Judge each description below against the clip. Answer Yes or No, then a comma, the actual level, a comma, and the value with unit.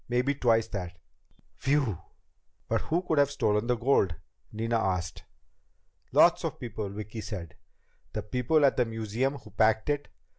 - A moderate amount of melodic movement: Yes, average, 4.5 semitones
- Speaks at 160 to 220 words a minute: No, average, 150 wpm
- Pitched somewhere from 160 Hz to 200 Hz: No, low, 115 Hz